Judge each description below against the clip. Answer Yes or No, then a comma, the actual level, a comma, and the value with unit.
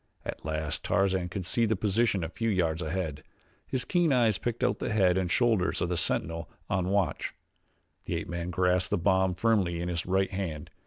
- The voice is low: Yes, very low, 95 Hz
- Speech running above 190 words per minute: Yes, average, 200 wpm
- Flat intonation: No, average, 3.1 semitones